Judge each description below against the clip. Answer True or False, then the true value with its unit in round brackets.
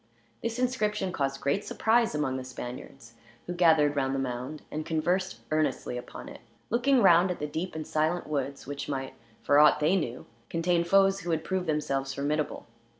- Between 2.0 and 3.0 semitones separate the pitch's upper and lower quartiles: False (4.8 semitones)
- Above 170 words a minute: True (180 wpm)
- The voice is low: False (155 Hz)